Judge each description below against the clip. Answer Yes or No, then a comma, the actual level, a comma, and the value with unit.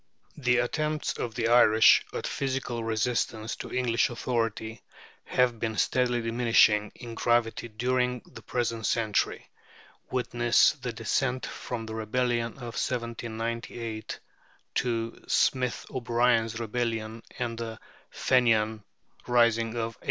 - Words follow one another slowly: Yes, slow, 115 wpm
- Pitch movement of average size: No, narrow, 1.6 semitones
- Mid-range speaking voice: No, low, 115 Hz